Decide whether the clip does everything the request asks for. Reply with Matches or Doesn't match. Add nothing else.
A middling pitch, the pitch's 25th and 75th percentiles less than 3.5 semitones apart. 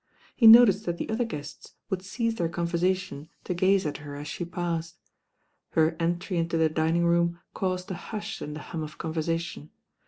Matches